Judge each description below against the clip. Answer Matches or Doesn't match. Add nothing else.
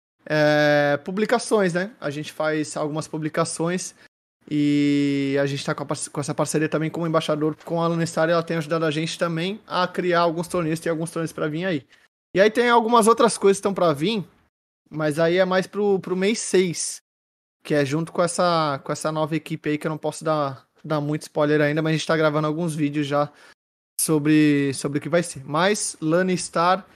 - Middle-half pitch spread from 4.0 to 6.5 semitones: Doesn't match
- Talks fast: Matches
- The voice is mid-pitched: Matches